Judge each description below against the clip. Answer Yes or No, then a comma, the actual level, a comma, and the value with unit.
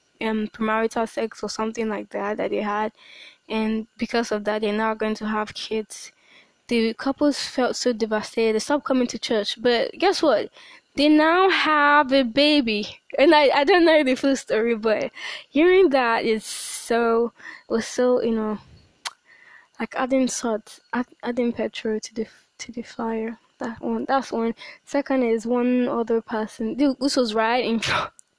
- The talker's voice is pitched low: No, high, 235 Hz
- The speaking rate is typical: Yes, average, 170 wpm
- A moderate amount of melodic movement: Yes, average, 3.5 semitones